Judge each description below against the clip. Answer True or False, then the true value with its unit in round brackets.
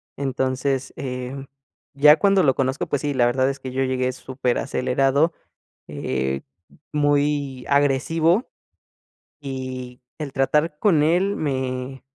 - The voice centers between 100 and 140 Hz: True (135 Hz)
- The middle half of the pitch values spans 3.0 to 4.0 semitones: False (2.4 semitones)